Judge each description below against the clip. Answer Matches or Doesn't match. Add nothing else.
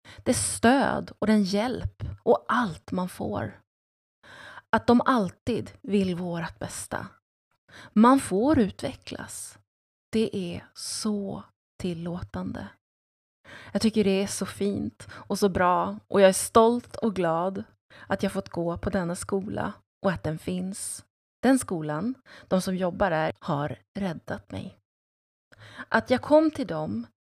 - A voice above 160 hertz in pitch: Matches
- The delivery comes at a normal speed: Matches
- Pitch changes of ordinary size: Doesn't match